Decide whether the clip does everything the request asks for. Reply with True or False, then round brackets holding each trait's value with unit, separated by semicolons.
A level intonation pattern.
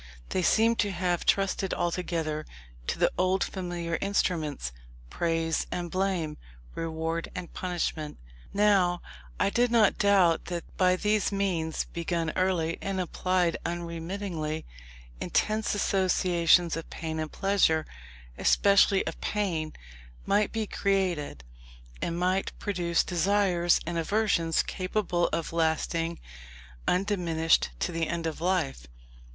False (3.0 semitones)